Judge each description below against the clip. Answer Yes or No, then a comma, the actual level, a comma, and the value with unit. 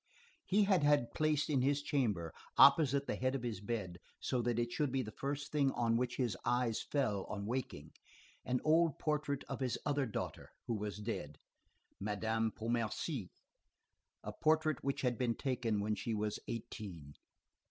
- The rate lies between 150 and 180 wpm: Yes, average, 170 wpm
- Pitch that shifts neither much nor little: Yes, average, 4.7 semitones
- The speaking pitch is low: Yes, low, 120 Hz